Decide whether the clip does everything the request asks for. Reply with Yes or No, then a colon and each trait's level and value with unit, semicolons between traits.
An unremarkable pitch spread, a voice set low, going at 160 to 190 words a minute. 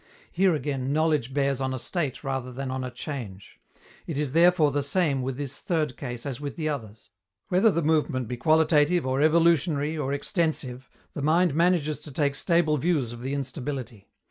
No: average, 3.5 semitones; medium, 145 Hz; average, 185 wpm